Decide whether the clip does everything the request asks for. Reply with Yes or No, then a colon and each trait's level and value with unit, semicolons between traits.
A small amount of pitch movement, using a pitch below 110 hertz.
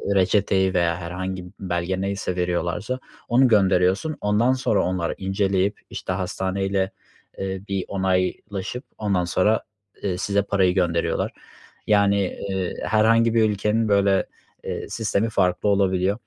Yes: narrow, 2.1 semitones; very low, 95 Hz